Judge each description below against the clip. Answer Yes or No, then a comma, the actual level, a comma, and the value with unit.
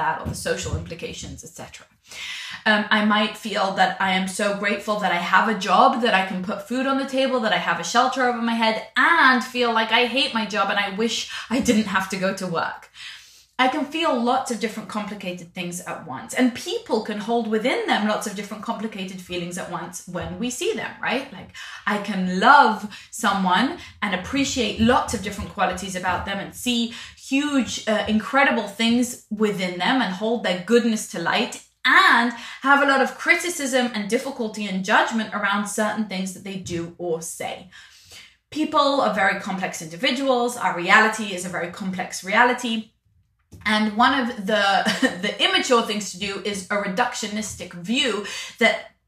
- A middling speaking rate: Yes, average, 185 wpm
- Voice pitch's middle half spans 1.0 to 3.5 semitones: No, average, 4.2 semitones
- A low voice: No, high, 215 Hz